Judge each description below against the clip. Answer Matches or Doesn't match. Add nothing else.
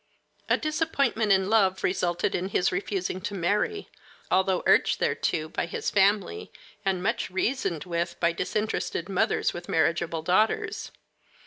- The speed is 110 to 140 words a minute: Matches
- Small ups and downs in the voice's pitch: Doesn't match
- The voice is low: Doesn't match